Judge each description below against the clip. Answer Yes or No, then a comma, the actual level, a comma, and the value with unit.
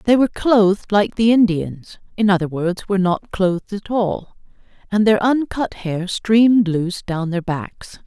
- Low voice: No, high, 200 Hz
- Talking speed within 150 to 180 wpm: Yes, average, 155 wpm